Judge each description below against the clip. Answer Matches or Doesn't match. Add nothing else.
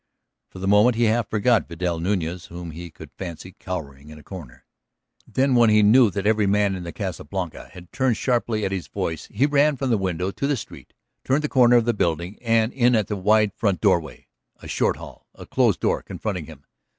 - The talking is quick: Matches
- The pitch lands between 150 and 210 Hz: Doesn't match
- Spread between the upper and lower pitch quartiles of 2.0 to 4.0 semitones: Doesn't match